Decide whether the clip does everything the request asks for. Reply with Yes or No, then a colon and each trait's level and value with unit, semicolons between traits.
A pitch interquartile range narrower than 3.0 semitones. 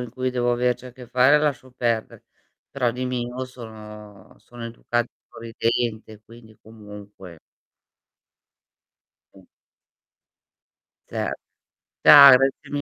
Yes: narrow, 2.6 semitones